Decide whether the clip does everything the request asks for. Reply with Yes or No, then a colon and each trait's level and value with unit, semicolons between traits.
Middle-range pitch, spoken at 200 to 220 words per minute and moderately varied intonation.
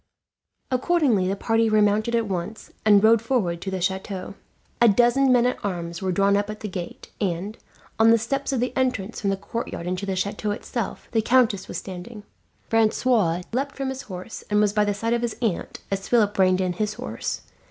No: high, 210 Hz; fast, 205 wpm; average, 3.7 semitones